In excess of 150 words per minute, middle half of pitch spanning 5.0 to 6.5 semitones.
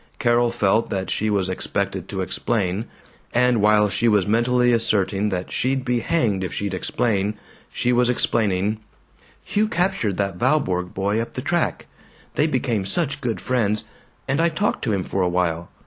No: average, 170 wpm; average, 4.1 semitones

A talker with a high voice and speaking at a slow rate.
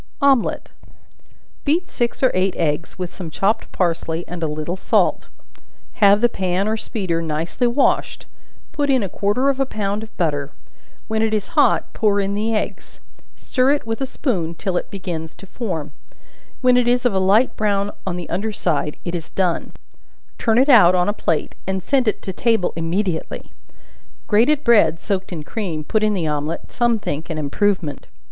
No: high, 195 Hz; average, 180 wpm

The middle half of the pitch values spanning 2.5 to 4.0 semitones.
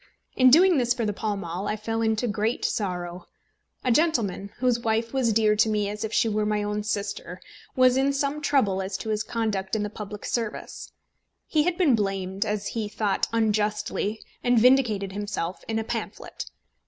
Yes: average, 2.8 semitones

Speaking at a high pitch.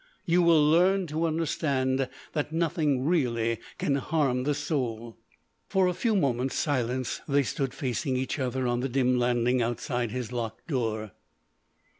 No: low, 130 Hz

